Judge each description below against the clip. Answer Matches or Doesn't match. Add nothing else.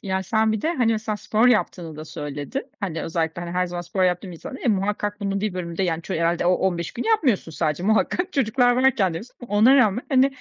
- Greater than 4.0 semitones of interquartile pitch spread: Matches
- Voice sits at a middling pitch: Doesn't match